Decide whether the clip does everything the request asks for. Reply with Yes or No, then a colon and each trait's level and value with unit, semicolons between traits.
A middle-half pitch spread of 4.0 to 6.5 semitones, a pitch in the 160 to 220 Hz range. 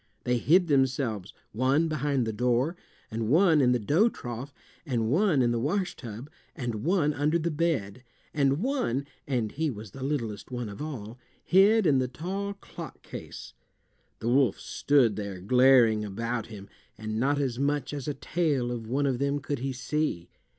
No: average, 4.4 semitones; low, 135 Hz